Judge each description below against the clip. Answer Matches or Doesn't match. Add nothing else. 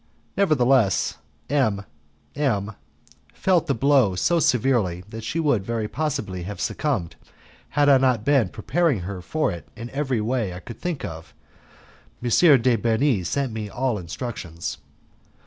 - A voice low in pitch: Matches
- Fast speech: Doesn't match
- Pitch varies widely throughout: Matches